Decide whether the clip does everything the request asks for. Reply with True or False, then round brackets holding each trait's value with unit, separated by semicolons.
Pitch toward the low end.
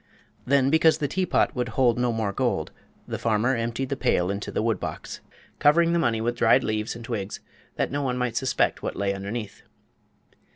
True (120 Hz)